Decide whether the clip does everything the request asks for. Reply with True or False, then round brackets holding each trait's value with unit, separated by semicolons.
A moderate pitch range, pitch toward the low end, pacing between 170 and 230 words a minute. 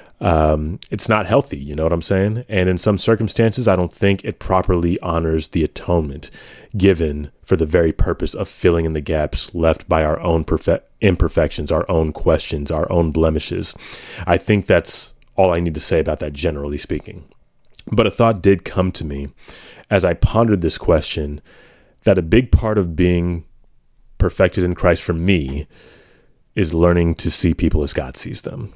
True (3.4 semitones; 85 Hz; 180 wpm)